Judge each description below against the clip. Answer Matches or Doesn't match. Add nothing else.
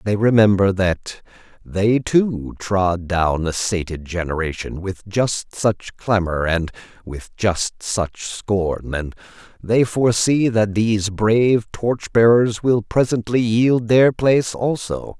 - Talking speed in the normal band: Doesn't match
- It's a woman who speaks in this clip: Doesn't match